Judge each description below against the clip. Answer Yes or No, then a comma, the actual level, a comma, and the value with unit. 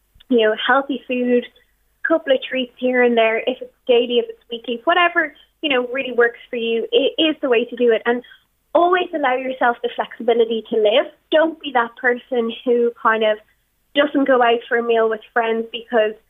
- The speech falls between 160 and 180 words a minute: No, fast, 205 wpm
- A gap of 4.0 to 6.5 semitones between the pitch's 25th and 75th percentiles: No, average, 2.8 semitones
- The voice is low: No, high, 245 Hz